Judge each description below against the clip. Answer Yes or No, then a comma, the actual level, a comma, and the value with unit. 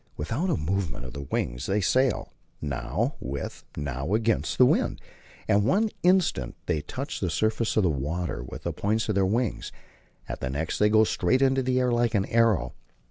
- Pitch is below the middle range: Yes, low, 105 Hz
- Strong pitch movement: Yes, wide, 8.2 semitones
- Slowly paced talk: No, average, 190 wpm